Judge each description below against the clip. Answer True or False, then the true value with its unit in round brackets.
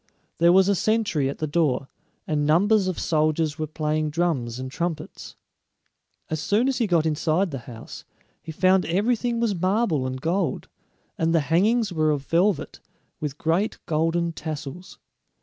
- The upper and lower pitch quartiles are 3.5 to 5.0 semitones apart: True (3.9 semitones)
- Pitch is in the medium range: True (165 Hz)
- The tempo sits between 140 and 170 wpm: True (160 wpm)